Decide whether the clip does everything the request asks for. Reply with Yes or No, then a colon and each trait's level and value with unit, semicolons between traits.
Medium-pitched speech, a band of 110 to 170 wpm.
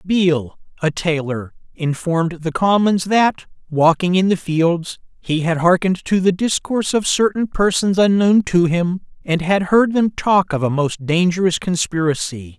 Yes: medium, 180 Hz; average, 155 wpm